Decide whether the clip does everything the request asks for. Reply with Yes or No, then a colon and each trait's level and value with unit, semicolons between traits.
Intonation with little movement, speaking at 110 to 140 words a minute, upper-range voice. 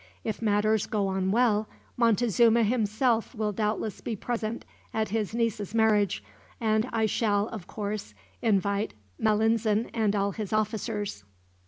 Yes: narrow, 1.6 semitones; slow, 135 wpm; high, 215 Hz